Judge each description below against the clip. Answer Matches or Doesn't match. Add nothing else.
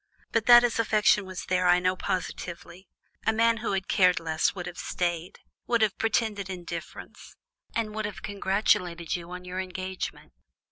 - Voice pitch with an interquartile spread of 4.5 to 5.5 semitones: Doesn't match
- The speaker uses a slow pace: Doesn't match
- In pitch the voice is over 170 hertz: Matches